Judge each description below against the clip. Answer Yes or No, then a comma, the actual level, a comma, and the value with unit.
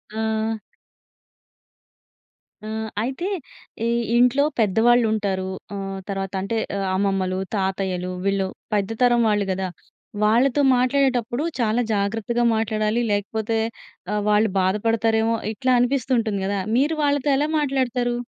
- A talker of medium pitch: No, high, 220 Hz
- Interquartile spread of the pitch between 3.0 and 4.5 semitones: Yes, average, 3.5 semitones